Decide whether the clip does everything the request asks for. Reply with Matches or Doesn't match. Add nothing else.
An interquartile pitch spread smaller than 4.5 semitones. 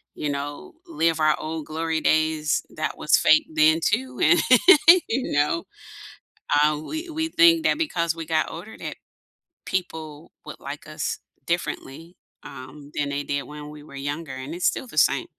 Matches